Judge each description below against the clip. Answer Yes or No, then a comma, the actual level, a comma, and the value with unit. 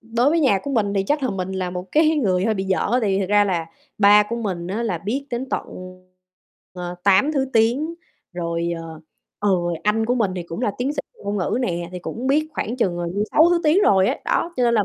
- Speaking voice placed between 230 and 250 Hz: No, high, 210 Hz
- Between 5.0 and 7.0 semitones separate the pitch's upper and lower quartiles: Yes, wide, 5.5 semitones